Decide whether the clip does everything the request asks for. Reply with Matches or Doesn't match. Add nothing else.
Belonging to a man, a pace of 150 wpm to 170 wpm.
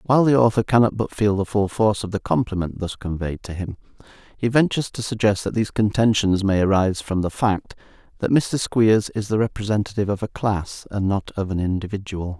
Doesn't match